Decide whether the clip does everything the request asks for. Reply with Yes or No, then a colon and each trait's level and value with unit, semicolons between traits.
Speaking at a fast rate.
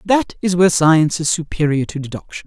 No: average, 195 wpm